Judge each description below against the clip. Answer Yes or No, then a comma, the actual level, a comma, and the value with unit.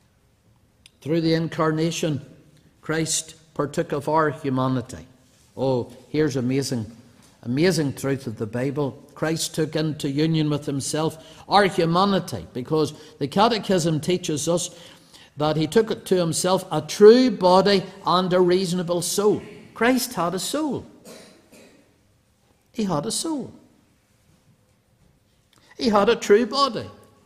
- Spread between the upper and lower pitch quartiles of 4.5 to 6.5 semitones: Yes, average, 4.8 semitones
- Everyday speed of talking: No, slow, 120 wpm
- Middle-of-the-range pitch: Yes, medium, 160 Hz